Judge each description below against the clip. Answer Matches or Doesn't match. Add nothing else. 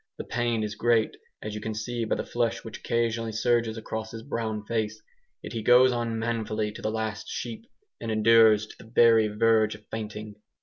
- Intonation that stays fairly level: Matches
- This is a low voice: Matches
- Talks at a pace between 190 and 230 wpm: Matches